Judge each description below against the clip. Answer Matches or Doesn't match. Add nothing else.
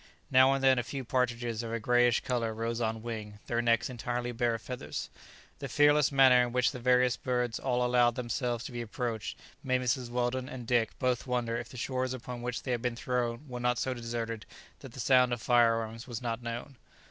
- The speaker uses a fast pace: Matches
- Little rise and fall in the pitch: Matches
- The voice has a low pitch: Matches